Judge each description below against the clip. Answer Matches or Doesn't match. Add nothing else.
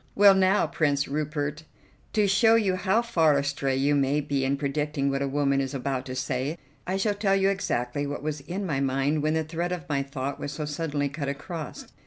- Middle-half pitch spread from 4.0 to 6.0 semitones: Matches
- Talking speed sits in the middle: Doesn't match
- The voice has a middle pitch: Matches